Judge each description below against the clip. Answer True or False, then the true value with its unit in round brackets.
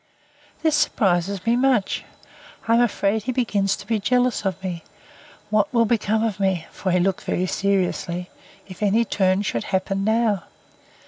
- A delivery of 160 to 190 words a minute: True (165 wpm)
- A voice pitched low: False (200 Hz)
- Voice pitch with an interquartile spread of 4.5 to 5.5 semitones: False (3.3 semitones)